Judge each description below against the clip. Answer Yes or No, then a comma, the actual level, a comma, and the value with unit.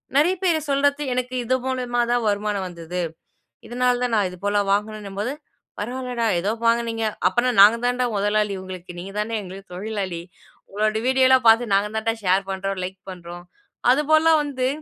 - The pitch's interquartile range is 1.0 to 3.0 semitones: No, average, 4.2 semitones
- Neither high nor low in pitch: No, high, 220 Hz